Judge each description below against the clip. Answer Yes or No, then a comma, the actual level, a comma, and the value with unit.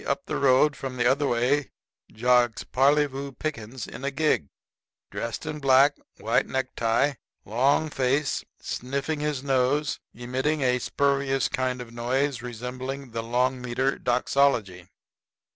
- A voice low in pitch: Yes, low, 130 Hz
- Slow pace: Yes, slow, 130 wpm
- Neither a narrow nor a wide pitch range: No, narrow, 2.3 semitones